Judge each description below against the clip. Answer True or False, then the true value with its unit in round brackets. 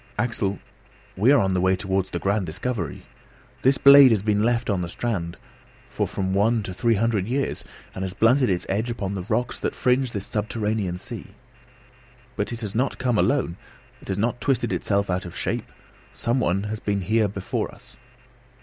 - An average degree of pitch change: True (3.9 semitones)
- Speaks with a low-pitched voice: True (105 Hz)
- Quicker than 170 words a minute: True (190 wpm)